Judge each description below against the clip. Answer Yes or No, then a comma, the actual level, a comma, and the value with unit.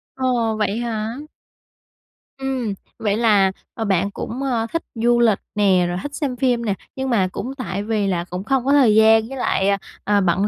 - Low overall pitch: No, high, 225 Hz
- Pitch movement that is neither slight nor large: Yes, average, 3.8 semitones